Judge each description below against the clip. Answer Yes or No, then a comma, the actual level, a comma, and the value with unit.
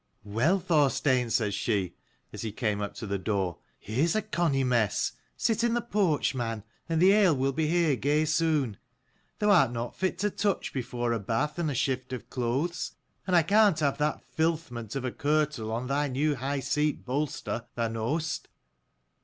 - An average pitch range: No, wide, 5.7 semitones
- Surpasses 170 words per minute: Yes, average, 185 wpm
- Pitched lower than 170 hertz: Yes, medium, 140 Hz